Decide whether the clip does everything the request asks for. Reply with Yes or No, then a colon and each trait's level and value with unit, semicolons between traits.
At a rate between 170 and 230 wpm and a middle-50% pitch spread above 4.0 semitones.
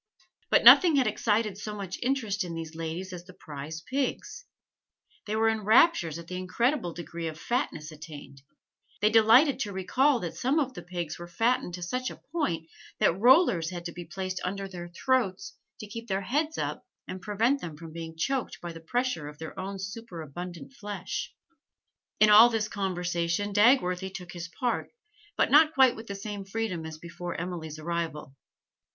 Yes: average, 180 wpm; average, 5.2 semitones